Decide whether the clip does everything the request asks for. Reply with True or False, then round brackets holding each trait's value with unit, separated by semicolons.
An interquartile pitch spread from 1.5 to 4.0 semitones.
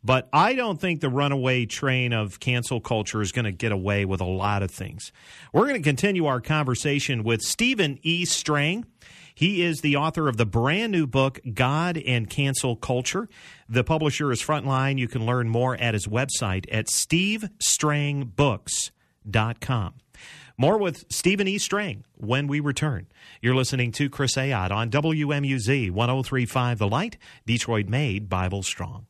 False (4.6 semitones)